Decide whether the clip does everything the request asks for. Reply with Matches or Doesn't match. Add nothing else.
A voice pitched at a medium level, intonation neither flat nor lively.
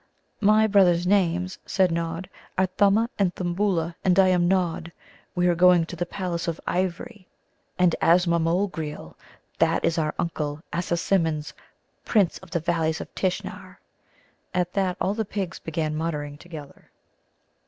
Doesn't match